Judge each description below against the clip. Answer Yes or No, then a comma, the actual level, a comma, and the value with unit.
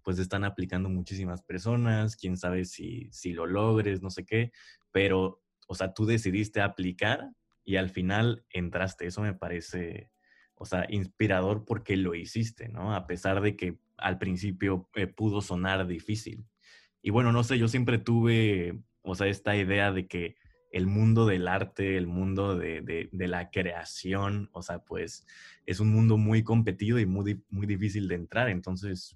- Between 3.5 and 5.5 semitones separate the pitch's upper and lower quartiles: No, average, 2.7 semitones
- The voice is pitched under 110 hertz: Yes, very low, 95 Hz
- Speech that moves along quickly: No, average, 170 wpm